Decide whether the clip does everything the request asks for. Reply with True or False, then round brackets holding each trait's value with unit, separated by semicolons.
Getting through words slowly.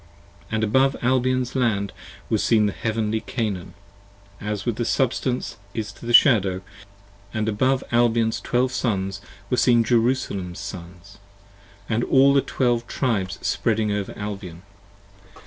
True (130 wpm)